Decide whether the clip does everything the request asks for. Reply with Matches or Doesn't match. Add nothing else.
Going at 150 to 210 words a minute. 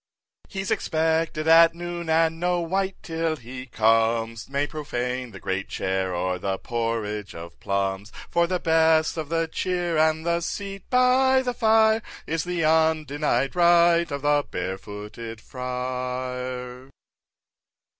Doesn't match